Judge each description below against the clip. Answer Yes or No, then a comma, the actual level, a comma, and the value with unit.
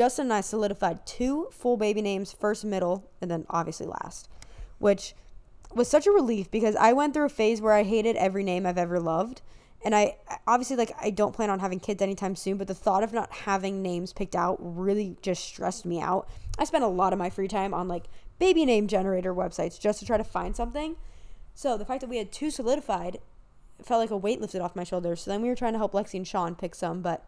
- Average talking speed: No, fast, 240 wpm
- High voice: Yes, high, 205 Hz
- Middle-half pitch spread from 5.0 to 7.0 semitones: No, average, 3.6 semitones